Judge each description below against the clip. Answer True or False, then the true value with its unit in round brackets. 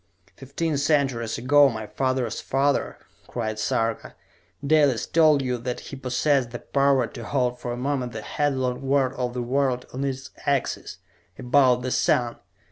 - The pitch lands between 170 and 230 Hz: False (130 Hz)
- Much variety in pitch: False (2.4 semitones)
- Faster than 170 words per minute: False (155 wpm)